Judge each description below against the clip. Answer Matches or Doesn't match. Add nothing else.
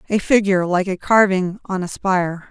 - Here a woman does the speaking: Matches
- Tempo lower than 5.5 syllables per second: Matches